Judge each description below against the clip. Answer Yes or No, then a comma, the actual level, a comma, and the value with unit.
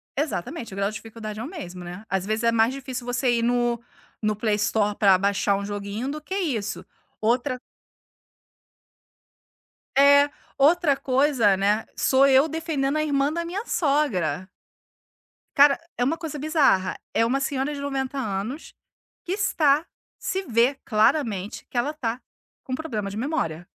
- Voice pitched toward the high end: Yes, very high, 255 Hz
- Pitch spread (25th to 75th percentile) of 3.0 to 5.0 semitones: No, wide, 5.4 semitones